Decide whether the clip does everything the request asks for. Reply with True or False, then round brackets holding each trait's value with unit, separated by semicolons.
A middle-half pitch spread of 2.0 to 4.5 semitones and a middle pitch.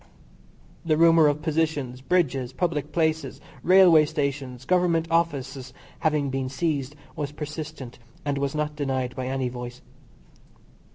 True (3.4 semitones; 145 Hz)